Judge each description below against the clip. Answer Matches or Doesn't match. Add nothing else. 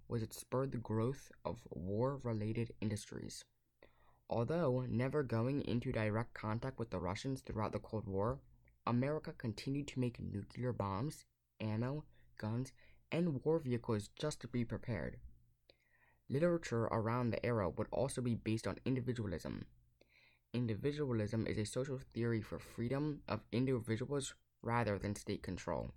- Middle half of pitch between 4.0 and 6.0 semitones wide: Doesn't match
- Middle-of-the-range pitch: Doesn't match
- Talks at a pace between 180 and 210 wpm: Doesn't match